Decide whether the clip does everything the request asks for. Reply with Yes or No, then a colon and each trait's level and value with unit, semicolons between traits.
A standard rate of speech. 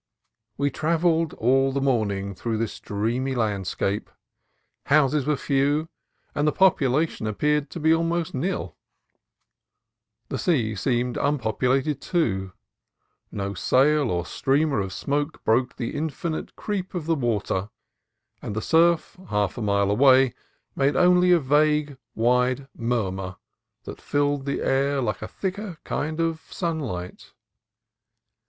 No: slow, 130 wpm